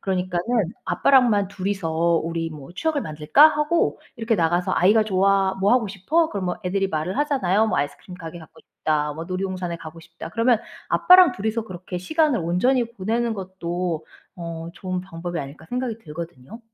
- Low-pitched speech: No, medium, 185 Hz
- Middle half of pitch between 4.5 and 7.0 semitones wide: Yes, average, 5.1 semitones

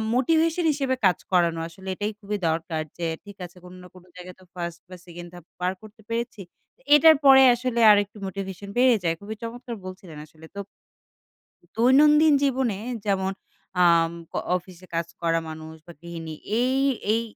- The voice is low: No, high, 190 Hz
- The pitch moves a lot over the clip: Yes, wide, 6.0 semitones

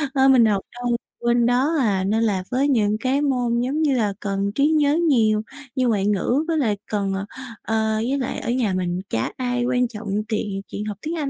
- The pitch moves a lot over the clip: No, average, 4.1 semitones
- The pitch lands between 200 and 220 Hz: No, high, 235 Hz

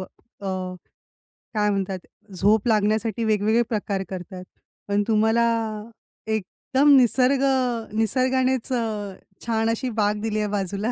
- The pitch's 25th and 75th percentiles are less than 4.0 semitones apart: Yes, narrow, 2.4 semitones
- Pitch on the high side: Yes, high, 220 Hz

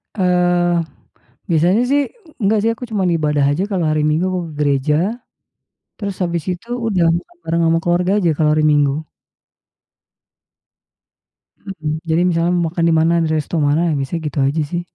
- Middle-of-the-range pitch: Yes, medium, 170 Hz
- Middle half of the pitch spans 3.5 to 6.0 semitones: No, average, 2.7 semitones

